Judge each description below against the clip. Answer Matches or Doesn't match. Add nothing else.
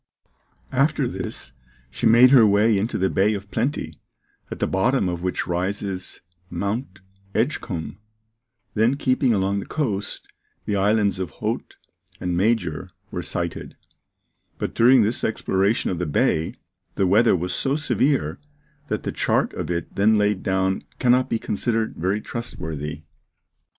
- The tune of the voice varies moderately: Matches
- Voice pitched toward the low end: Matches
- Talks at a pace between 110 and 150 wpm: Matches